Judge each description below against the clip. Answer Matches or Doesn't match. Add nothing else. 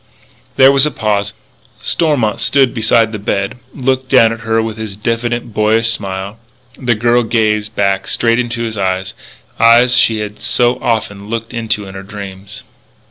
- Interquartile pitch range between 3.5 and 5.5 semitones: Doesn't match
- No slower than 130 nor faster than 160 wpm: Doesn't match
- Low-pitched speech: Matches